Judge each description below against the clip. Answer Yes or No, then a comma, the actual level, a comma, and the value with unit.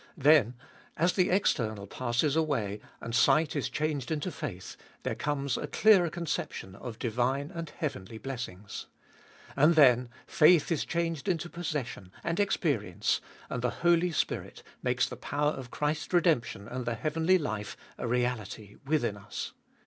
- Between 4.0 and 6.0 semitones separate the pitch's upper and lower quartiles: Yes, wide, 5.6 semitones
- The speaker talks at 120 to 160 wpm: Yes, average, 150 wpm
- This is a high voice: No, medium, 140 Hz